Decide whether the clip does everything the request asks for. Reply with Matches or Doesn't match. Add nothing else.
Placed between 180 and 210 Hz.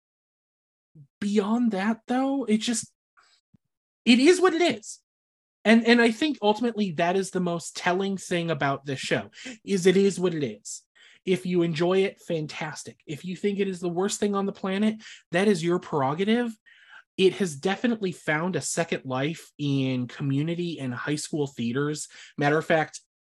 Matches